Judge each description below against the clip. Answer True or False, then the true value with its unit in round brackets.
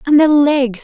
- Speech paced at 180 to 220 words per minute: True (215 wpm)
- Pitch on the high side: True (275 Hz)